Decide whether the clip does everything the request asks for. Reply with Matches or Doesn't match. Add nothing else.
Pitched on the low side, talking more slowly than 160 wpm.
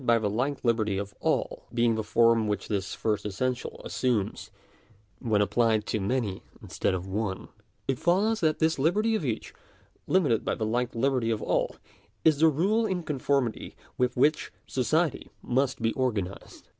Doesn't match